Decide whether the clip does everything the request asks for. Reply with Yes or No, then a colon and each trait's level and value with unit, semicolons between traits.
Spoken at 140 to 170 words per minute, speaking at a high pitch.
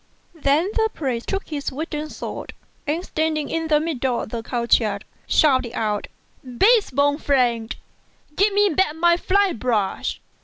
Yes: average, 155 wpm; very high, 295 Hz